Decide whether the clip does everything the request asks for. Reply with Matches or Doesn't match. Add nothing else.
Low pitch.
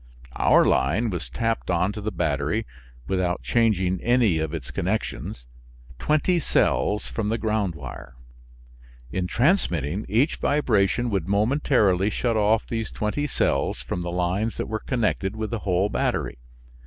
Matches